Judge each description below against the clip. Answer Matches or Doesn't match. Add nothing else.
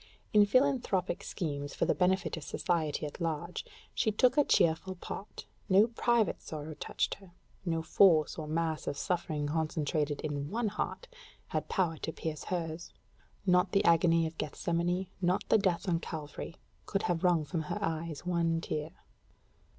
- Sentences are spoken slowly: Doesn't match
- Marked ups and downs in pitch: Doesn't match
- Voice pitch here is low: Doesn't match